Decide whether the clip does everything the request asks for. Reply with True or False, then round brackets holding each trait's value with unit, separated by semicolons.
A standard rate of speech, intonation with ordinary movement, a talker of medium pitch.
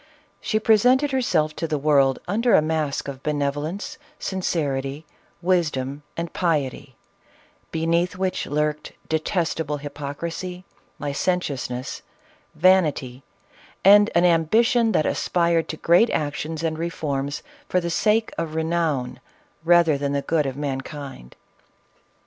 False (120 wpm; 3.8 semitones; 160 Hz)